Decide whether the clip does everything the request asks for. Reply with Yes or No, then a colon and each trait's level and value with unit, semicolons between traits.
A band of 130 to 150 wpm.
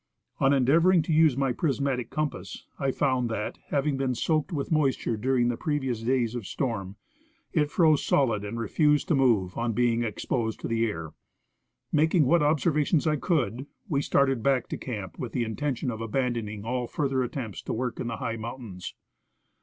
No: average, 180 wpm